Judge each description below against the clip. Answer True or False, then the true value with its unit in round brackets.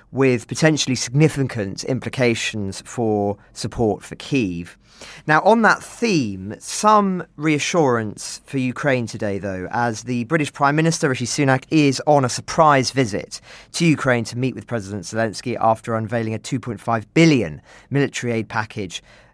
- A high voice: False (125 Hz)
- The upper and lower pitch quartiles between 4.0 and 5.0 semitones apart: True (4.7 semitones)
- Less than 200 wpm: True (140 wpm)